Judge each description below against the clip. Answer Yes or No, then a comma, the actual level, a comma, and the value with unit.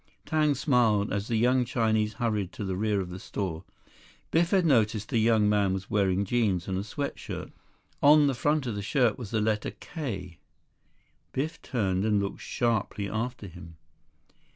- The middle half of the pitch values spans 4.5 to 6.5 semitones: No, average, 3.9 semitones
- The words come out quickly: No, average, 175 wpm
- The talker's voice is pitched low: Yes, low, 110 Hz